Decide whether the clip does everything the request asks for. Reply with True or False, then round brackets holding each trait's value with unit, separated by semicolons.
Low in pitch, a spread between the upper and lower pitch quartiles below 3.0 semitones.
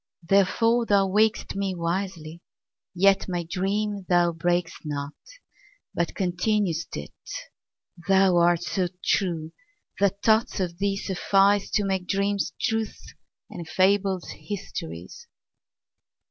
False (190 Hz; 2.6 semitones)